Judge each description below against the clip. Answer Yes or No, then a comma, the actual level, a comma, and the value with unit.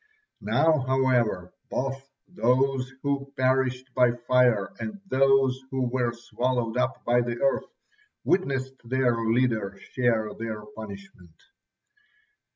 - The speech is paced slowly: Yes, slow, 110 wpm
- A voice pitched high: No, low, 125 Hz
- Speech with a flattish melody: Yes, narrow, 2.2 semitones